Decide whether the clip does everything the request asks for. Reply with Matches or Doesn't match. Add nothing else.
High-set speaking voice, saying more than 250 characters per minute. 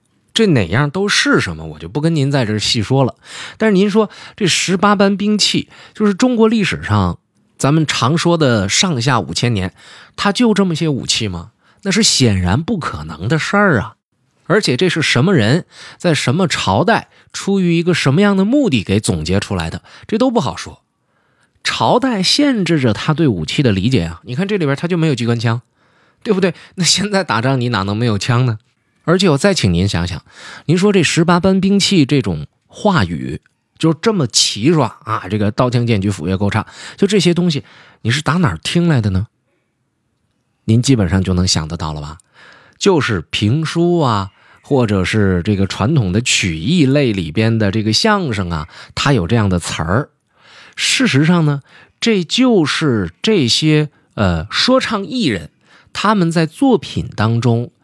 Doesn't match